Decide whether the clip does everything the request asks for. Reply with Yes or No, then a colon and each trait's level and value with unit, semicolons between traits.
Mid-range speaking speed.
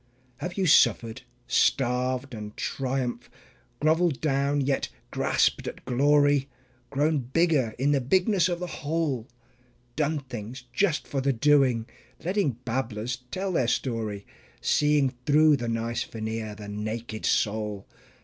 No: slow, 130 wpm